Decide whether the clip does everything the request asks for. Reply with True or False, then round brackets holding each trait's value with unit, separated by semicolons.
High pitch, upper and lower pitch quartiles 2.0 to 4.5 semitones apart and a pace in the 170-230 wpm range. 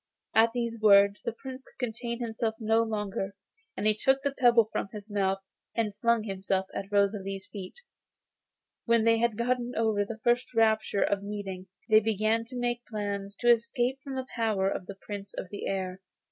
True (220 Hz; 2.7 semitones; 180 wpm)